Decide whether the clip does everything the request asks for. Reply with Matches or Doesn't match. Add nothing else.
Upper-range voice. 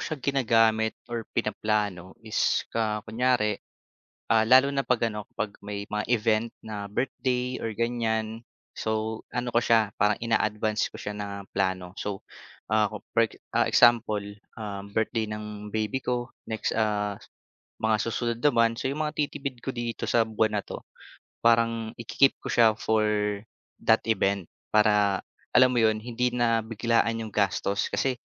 Doesn't match